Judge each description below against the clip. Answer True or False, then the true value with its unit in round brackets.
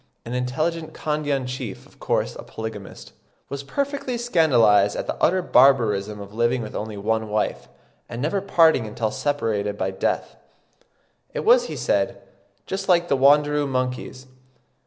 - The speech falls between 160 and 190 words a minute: False (150 wpm)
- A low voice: True (130 Hz)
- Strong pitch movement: True (6.3 semitones)